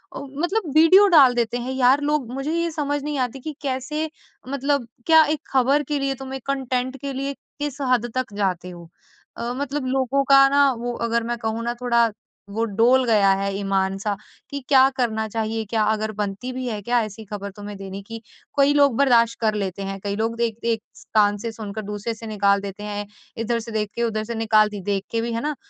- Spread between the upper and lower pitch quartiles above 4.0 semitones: Yes, average, 4.4 semitones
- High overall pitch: Yes, high, 235 Hz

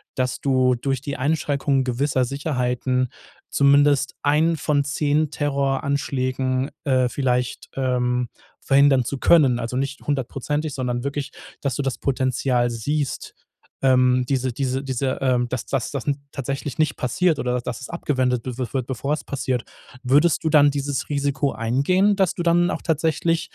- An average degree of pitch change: No, narrow, 2.2 semitones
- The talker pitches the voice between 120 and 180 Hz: Yes, low, 135 Hz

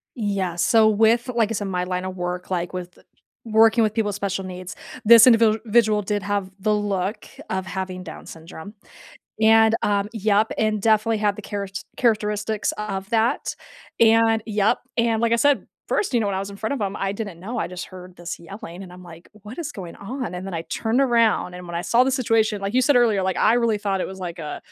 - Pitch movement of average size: Yes, average, 3.1 semitones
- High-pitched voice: Yes, high, 210 Hz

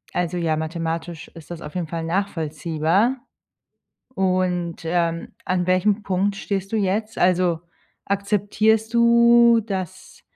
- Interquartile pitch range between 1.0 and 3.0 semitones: No, average, 3.5 semitones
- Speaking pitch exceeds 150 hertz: Yes, medium, 185 Hz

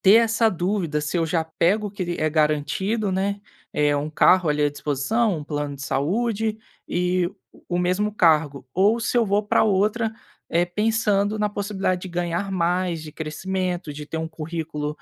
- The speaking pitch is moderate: Yes, medium, 180 Hz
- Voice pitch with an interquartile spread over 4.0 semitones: Yes, average, 4.8 semitones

